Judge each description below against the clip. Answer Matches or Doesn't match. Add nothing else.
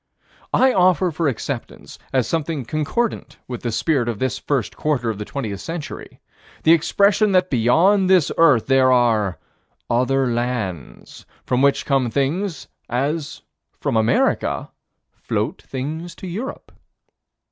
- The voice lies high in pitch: Doesn't match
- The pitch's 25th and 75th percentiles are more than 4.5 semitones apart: Matches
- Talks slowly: Matches